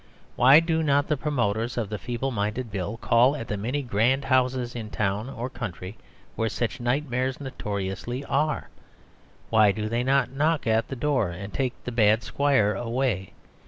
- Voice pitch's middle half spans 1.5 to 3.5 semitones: No, average, 3.9 semitones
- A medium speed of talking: Yes, average, 170 wpm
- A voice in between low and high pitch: No, low, 120 Hz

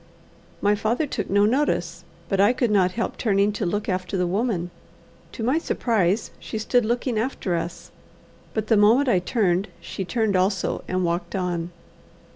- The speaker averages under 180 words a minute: Yes, average, 170 wpm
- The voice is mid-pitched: No, high, 205 Hz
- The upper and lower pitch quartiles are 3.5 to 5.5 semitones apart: Yes, average, 3.9 semitones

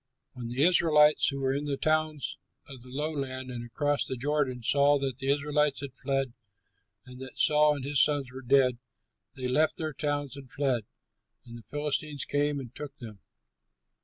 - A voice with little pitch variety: Yes, narrow, 2.3 semitones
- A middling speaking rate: Yes, average, 180 wpm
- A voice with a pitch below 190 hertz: Yes, medium, 140 Hz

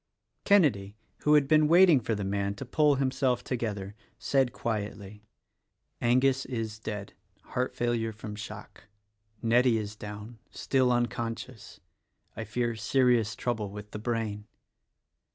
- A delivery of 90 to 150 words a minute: Yes, average, 145 wpm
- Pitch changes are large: No, average, 3.6 semitones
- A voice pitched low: Yes, low, 115 Hz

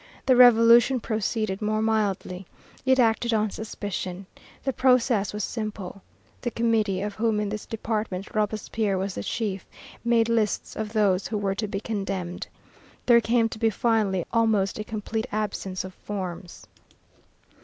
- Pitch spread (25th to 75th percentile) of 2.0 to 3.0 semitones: Yes, narrow, 2.6 semitones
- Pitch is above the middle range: Yes, high, 215 Hz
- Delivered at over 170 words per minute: No, average, 150 wpm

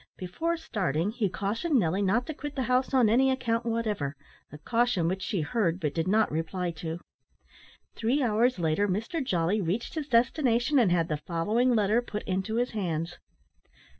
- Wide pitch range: Yes, wide, 5.7 semitones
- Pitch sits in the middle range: No, high, 210 Hz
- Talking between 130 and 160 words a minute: No, average, 175 wpm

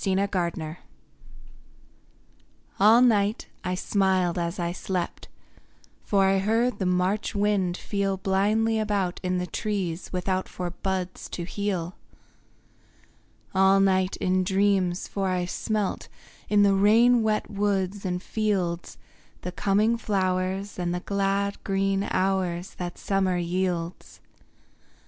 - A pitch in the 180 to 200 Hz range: Yes, high, 190 Hz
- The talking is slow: Yes, slow, 120 wpm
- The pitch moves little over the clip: Yes, narrow, 2.0 semitones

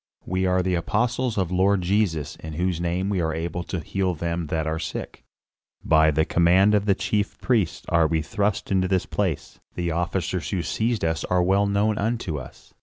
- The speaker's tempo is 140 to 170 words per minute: No, average, 200 wpm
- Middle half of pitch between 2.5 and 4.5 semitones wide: Yes, average, 3.5 semitones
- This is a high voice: No, very low, 90 Hz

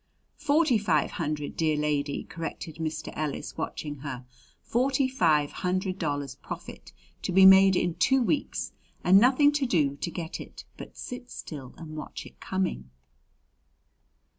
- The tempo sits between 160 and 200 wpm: No, average, 145 wpm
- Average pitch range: No, wide, 6.5 semitones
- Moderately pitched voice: Yes, medium, 170 Hz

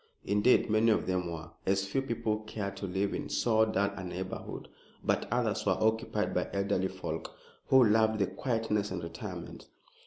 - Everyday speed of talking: Yes, average, 175 wpm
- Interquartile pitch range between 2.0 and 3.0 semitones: Yes, average, 2.7 semitones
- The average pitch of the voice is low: Yes, low, 100 Hz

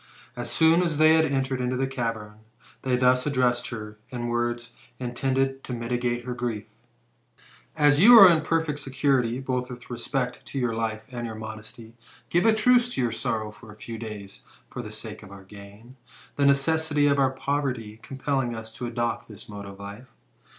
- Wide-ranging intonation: No, average, 3.4 semitones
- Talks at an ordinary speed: Yes, average, 185 wpm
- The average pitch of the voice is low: Yes, low, 125 Hz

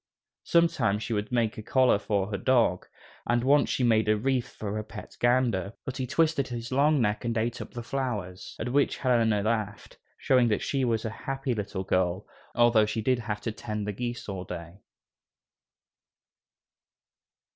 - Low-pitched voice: Yes, low, 115 Hz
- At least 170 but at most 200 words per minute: Yes, average, 180 wpm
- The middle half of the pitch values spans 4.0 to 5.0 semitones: No, average, 3.5 semitones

